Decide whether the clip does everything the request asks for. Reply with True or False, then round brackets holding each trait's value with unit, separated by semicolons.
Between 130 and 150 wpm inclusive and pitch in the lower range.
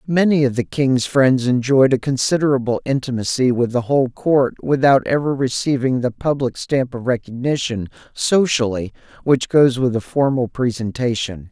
True (145 wpm; 130 Hz)